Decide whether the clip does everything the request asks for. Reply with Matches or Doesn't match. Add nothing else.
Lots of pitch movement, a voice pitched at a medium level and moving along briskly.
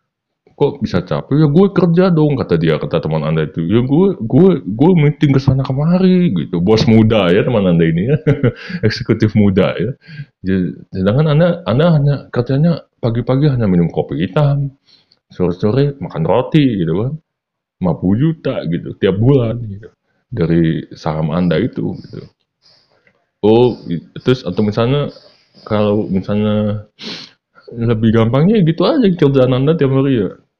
Doesn't match